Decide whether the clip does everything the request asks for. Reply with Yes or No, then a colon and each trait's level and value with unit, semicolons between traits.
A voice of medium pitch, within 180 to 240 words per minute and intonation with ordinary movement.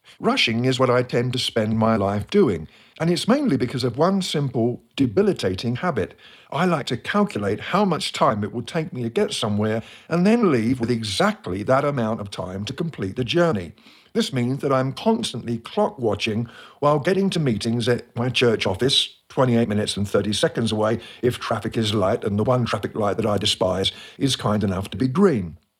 No: low, 120 Hz; average, 200 wpm; average, 4.8 semitones